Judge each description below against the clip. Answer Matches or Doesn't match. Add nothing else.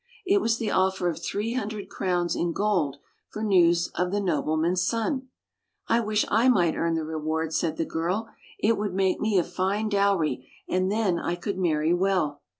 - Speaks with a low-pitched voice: Doesn't match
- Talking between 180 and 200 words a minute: Matches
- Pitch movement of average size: Matches